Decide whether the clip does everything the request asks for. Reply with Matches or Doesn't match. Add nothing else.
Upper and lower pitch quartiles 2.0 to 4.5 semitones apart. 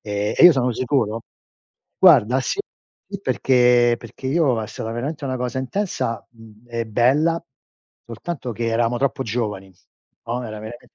Matches